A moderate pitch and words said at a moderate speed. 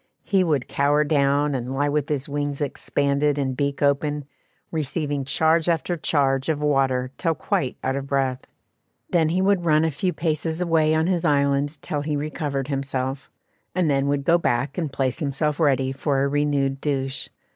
Yes: medium, 145 Hz; average, 180 wpm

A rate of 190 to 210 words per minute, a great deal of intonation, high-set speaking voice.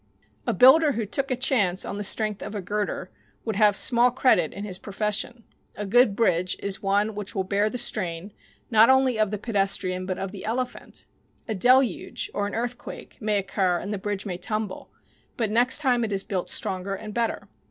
No: average, 200 wpm; average, 3.3 semitones; high, 210 Hz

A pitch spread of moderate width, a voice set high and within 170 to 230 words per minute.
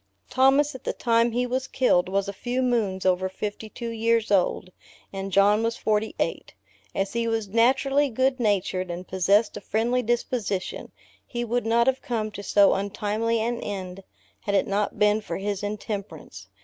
Yes: average, 3.3 semitones; high, 215 Hz; average, 175 wpm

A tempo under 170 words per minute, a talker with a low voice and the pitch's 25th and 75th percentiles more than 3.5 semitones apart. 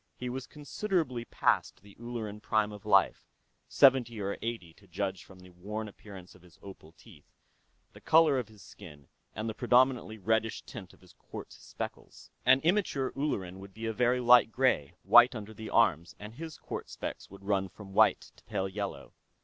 No: average, 185 wpm; low, 110 Hz; average, 4.2 semitones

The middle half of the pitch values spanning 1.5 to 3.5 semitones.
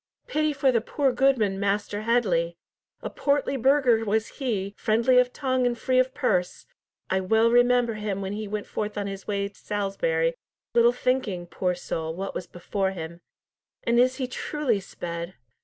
No: average, 4.5 semitones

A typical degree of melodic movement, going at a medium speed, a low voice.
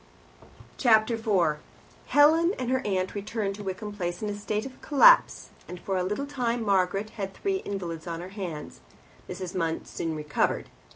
No: average, 4.3 semitones; average, 170 wpm; high, 200 Hz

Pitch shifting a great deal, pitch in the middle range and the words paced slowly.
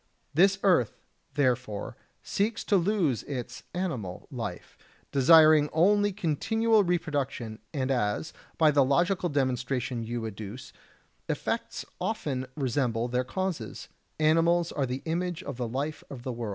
Yes: wide, 5.9 semitones; medium, 145 Hz; slow, 130 wpm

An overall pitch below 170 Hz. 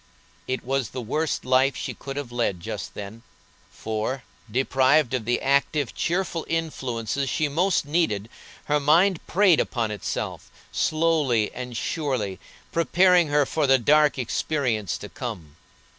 Yes: low, 135 Hz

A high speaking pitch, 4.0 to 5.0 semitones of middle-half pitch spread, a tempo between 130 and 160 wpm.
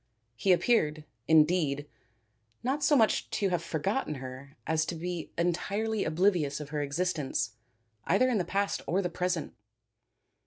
No: medium, 170 Hz; average, 4.7 semitones; average, 145 wpm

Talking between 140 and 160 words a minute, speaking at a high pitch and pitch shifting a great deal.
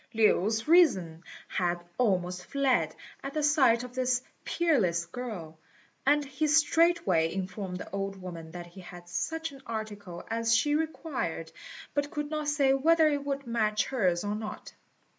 Yes: average, 155 wpm; high, 230 Hz; wide, 8.0 semitones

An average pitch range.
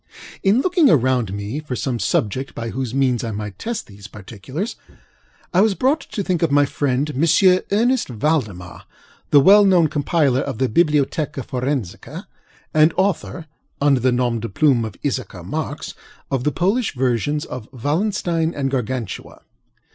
No: wide, 5.7 semitones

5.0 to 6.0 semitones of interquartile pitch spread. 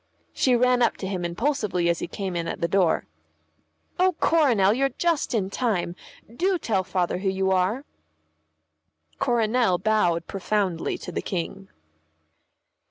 Yes: wide, 5.4 semitones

